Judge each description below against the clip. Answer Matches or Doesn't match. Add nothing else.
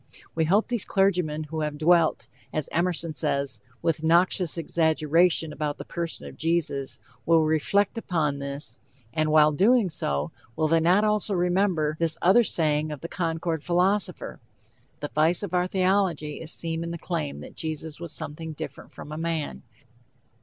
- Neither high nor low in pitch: Matches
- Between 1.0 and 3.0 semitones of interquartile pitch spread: Matches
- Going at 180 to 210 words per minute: Doesn't match